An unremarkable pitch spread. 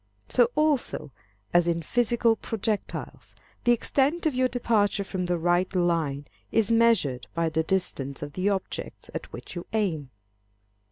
No: wide, 5.8 semitones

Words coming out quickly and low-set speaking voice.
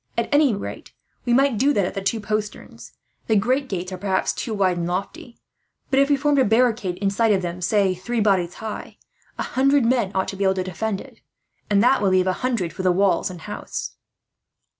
No: fast, 220 wpm; high, 205 Hz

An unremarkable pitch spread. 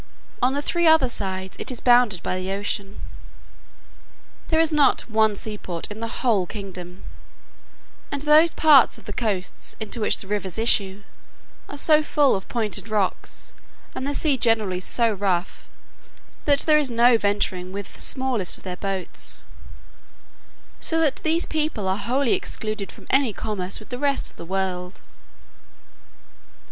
No: wide, 5.9 semitones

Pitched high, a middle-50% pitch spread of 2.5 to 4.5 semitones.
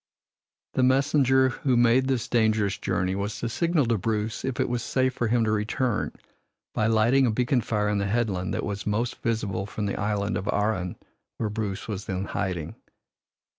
No: low, 110 Hz; average, 3.2 semitones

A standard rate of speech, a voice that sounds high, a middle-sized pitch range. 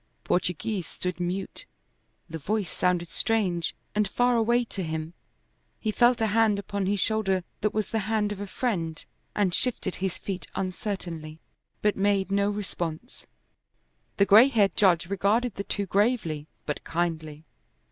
Yes: average, 150 wpm; high, 200 Hz; average, 3.6 semitones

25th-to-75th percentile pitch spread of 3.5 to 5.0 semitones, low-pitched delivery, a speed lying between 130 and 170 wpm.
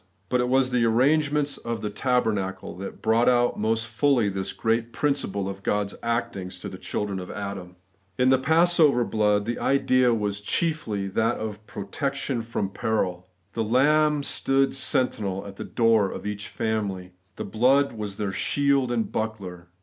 Yes: average, 4.3 semitones; low, 115 Hz; average, 165 wpm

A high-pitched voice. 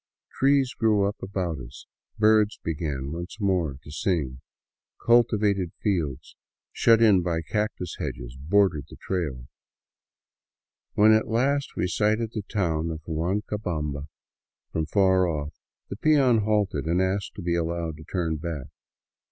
No: very low, 90 Hz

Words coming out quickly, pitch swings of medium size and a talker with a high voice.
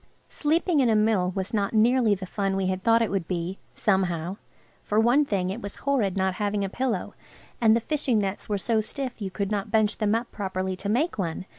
Yes: fast, 220 wpm; average, 3.3 semitones; high, 205 Hz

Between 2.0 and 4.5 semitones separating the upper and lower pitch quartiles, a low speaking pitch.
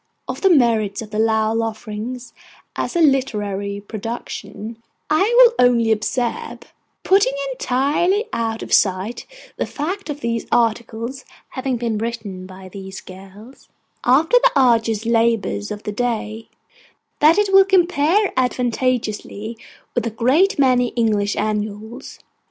No: average, 4.2 semitones; high, 230 Hz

